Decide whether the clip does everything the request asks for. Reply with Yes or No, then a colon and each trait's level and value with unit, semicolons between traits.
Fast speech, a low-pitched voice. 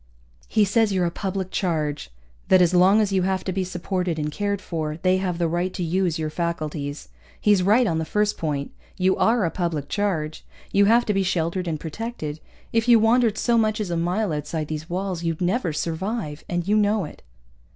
No: fast, 210 wpm; medium, 180 Hz